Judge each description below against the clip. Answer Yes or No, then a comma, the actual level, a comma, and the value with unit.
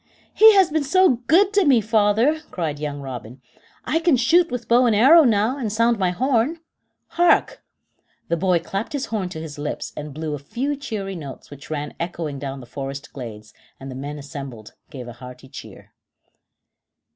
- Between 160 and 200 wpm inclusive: Yes, average, 185 wpm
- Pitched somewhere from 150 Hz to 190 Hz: Yes, medium, 185 Hz